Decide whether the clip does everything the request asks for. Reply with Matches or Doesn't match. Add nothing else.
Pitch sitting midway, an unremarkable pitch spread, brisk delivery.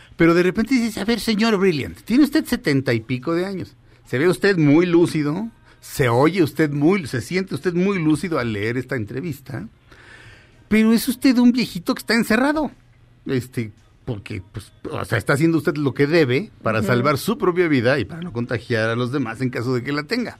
Doesn't match